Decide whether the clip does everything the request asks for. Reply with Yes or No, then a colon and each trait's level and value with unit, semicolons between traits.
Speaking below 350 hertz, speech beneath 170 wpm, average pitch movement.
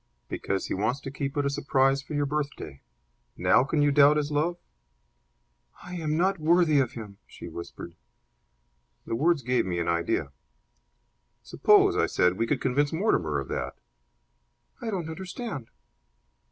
No: medium, 140 Hz; average, 155 wpm; wide, 5.7 semitones